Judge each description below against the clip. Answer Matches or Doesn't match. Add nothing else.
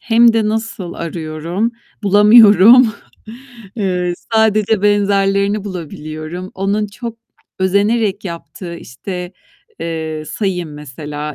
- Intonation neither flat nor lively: Matches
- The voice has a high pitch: Matches